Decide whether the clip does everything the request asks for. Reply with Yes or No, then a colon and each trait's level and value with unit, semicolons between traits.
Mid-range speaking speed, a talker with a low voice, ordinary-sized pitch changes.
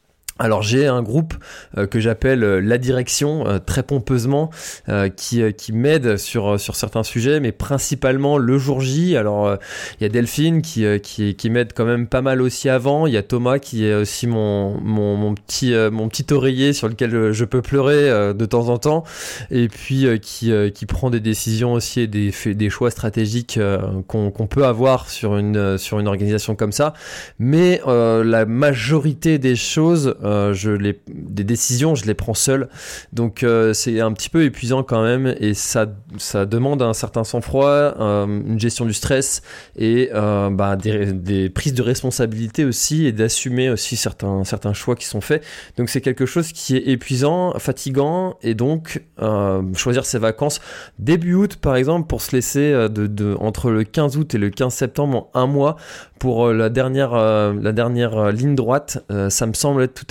Yes: average, 195 wpm; low, 120 Hz; average, 4.1 semitones